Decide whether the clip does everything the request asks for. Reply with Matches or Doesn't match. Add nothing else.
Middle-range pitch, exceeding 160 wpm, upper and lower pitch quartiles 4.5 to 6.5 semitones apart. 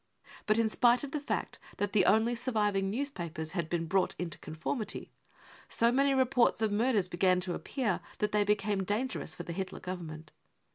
Doesn't match